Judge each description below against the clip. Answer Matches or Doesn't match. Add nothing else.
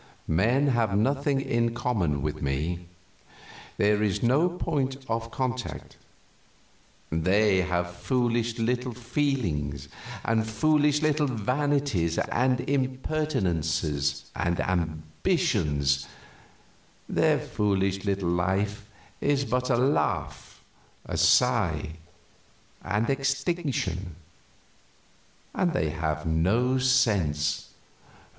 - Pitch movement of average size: Doesn't match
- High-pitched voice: Doesn't match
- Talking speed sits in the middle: Doesn't match